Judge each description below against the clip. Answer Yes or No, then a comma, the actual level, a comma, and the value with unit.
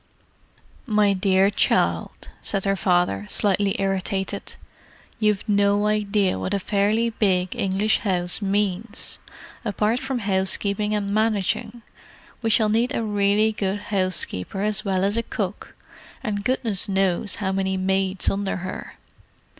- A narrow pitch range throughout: Yes, narrow, 1.8 semitones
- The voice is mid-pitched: No, high, 200 Hz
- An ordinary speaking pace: No, slow, 130 wpm